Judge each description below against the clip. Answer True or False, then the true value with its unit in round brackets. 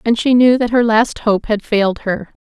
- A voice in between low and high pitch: False (220 Hz)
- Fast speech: True (245 wpm)